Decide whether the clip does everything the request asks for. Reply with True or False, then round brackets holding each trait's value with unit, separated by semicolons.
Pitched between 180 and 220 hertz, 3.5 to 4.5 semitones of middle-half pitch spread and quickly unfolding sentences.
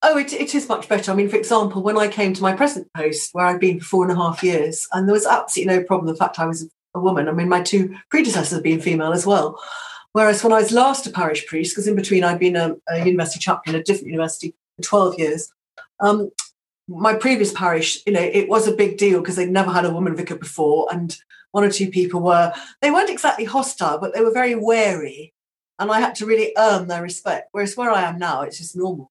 True (190 Hz; 4.0 semitones; 250 wpm)